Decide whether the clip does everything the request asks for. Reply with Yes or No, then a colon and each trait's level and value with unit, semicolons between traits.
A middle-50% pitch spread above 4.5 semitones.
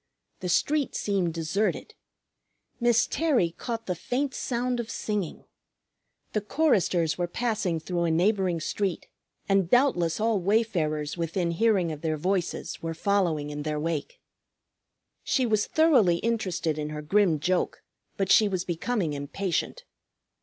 Yes: average, 5.2 semitones